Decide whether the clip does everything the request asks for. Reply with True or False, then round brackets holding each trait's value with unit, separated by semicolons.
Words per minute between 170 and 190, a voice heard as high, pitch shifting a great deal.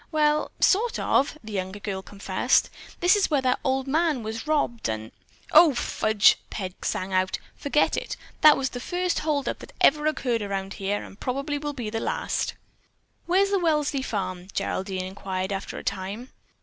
True (175 wpm; 250 Hz; 7.5 semitones)